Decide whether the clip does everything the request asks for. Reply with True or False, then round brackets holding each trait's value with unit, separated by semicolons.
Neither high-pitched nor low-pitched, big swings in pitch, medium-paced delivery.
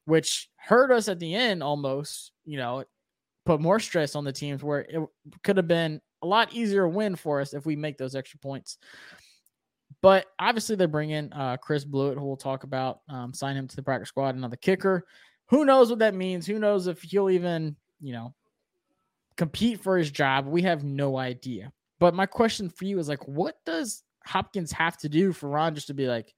False (160 Hz; 5.7 semitones; 210 wpm)